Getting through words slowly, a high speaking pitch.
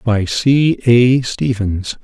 No: slow, 120 wpm; low, 115 Hz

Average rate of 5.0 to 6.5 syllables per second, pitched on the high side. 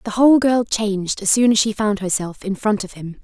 Yes: 5.5 syllables/s; high, 210 Hz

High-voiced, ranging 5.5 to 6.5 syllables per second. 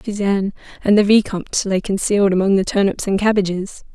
Yes: high, 200 Hz; 6.1 syllables/s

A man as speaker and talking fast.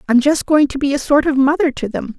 No: female; fast, 300 wpm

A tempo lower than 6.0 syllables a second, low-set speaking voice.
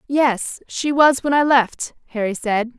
No: 3.9 syllables/s; very high, 255 Hz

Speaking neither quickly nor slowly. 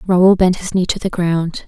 No: fast, 250 wpm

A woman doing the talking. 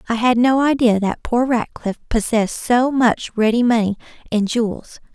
Yes: female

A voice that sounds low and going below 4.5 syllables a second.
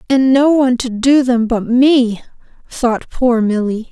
No: high, 245 Hz; 4.0 syllables/s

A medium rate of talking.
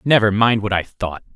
No: fast, 220 wpm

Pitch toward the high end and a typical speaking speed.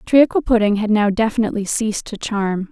Yes: high, 215 Hz; average, 175 wpm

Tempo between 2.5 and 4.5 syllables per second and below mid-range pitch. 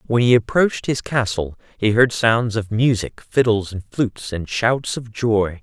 Yes: 4.4 syllables/s; low, 110 Hz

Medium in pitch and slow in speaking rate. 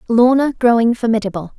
No: high, 230 Hz; slow, 115 wpm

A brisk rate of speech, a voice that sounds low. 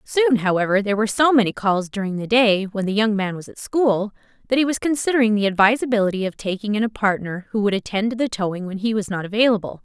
No: fast, 240 wpm; high, 215 Hz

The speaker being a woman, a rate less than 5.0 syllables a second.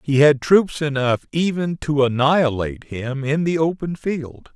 No: male; 4.4 syllables/s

